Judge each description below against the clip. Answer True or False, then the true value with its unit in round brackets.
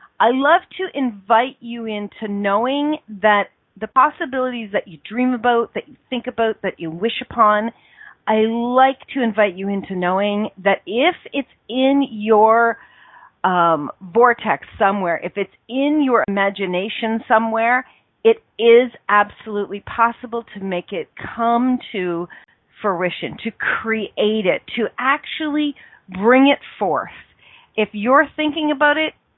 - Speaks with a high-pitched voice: True (230 Hz)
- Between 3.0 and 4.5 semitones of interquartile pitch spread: True (4.1 semitones)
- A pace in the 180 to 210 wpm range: False (135 wpm)